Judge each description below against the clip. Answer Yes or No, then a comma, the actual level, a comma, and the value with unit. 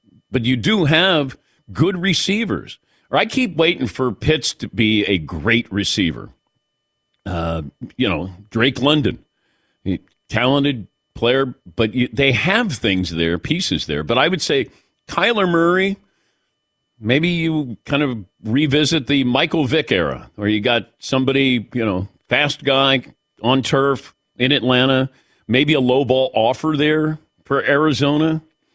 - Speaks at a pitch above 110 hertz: Yes, low, 135 Hz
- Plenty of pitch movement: No, average, 4.6 semitones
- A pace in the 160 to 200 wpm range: No, average, 140 wpm